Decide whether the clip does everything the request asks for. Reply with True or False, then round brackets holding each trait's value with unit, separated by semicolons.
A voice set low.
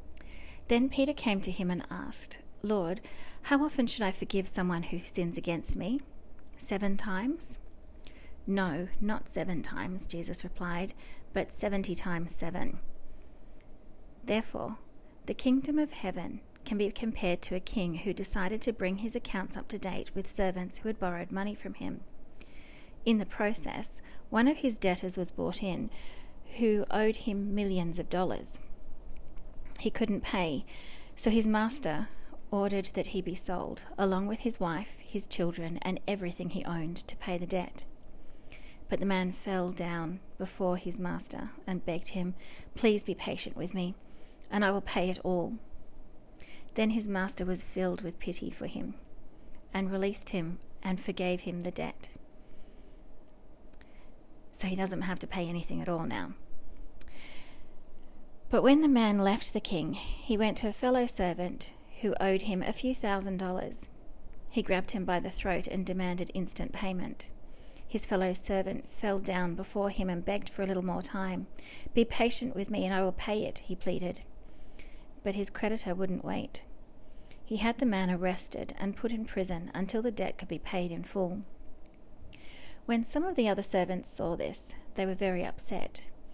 False (190 Hz)